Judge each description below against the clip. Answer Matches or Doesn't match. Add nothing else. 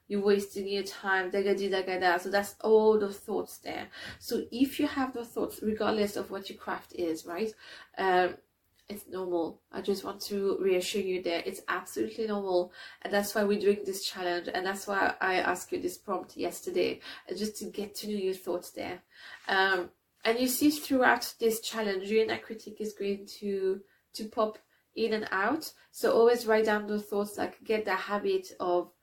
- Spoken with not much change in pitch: Matches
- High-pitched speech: Matches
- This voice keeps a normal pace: Matches